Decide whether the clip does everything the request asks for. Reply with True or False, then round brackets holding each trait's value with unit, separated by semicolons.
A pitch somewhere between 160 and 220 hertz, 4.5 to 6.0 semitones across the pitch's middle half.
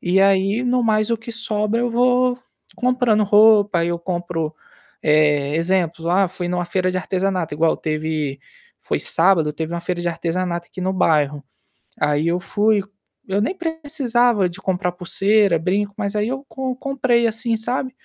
True (190 Hz; 5.0 semitones)